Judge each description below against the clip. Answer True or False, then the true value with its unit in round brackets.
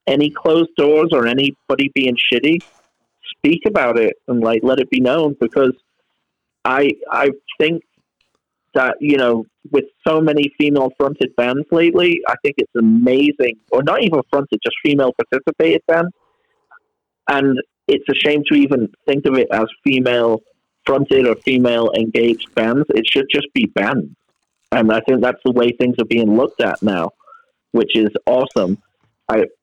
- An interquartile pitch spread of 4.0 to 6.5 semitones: True (5.3 semitones)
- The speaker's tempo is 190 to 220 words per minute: False (160 wpm)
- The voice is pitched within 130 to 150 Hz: True (140 Hz)